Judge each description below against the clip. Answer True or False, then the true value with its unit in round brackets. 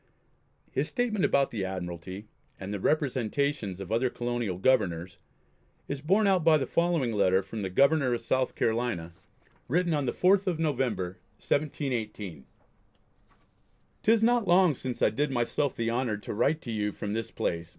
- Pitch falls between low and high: False (120 Hz)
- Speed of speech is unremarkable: True (165 wpm)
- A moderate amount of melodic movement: False (6.9 semitones)